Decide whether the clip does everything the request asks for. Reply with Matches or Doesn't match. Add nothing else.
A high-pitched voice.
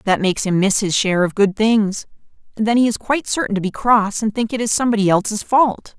Matches